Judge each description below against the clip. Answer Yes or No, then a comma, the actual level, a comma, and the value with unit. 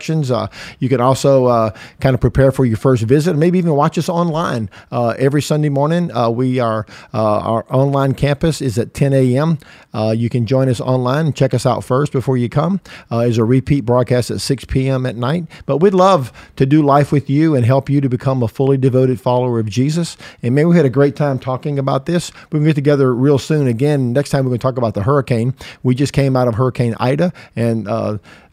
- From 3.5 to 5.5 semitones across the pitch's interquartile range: No, average, 2.8 semitones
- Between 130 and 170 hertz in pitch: Yes, low, 135 Hz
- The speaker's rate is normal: No, fast, 225 wpm